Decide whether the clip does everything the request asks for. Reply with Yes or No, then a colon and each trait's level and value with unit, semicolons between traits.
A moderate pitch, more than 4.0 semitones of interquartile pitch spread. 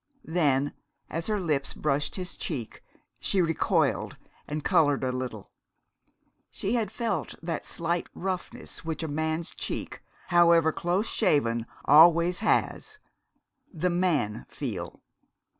No: medium, 165 Hz; average, 3.6 semitones